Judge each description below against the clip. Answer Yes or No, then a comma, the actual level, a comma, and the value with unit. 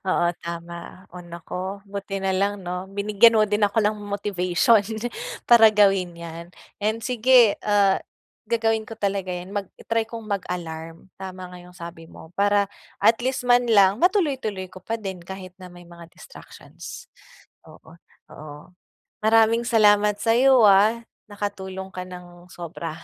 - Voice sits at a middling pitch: No, high, 195 Hz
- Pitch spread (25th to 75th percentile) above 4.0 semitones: No, average, 3.4 semitones